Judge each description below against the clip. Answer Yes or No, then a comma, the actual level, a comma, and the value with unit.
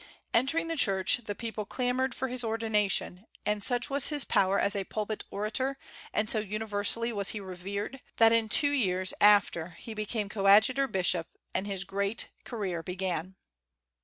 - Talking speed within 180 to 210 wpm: No, average, 160 wpm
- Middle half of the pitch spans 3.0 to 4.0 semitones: Yes, average, 3.4 semitones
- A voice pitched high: Yes, high, 210 Hz